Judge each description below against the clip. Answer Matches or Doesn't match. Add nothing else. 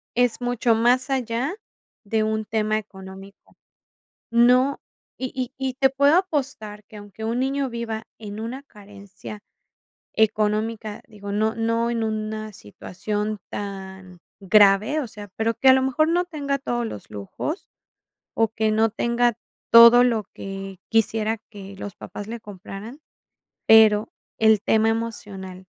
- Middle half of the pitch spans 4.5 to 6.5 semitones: Doesn't match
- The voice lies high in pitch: Matches